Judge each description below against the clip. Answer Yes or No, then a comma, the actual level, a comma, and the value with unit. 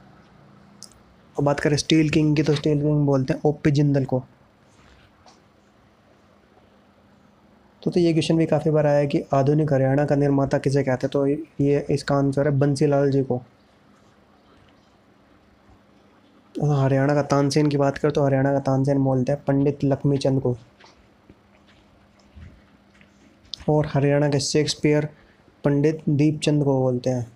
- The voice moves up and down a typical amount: No, narrow, 2.0 semitones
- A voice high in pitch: No, medium, 140 Hz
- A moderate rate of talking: Yes, average, 140 wpm